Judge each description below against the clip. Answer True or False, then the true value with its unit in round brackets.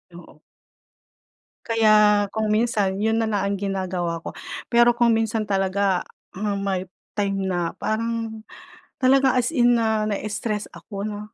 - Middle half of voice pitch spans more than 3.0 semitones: False (2.5 semitones)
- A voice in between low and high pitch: False (210 Hz)